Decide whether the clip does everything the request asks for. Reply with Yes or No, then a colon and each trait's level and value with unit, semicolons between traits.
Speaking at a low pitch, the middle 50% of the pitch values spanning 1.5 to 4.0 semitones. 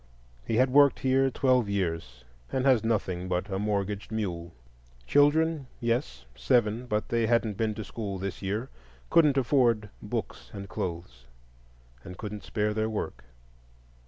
No: low, 105 Hz; average, 5.0 semitones